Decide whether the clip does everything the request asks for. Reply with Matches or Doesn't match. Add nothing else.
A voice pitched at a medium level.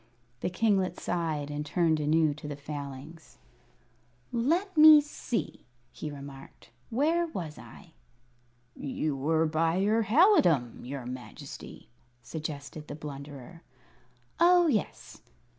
Matches